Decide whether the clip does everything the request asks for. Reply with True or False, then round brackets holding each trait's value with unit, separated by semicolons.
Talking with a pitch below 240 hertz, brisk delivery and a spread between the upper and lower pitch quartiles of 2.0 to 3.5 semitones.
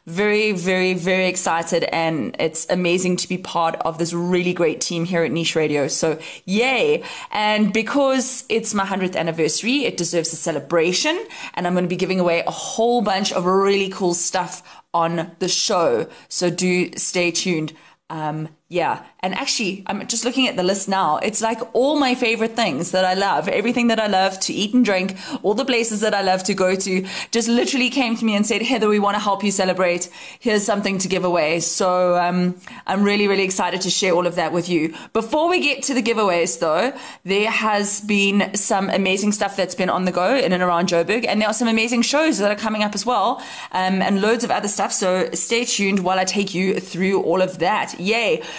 False (190 Hz; 215 wpm; 3.9 semitones)